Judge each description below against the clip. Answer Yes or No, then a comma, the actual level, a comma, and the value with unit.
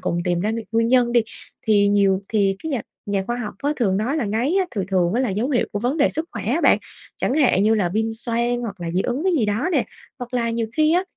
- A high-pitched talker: Yes, high, 230 Hz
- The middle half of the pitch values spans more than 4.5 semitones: No, average, 3.8 semitones